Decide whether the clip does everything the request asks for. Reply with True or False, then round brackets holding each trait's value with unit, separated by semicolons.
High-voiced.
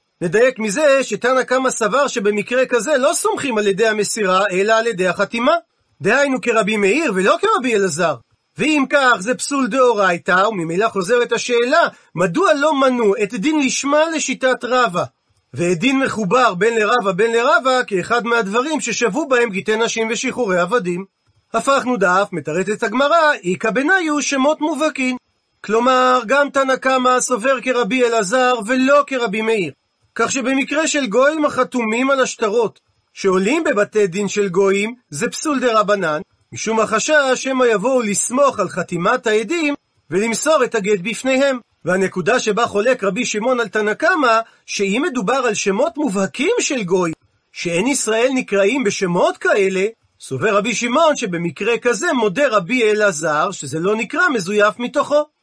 True (235 Hz)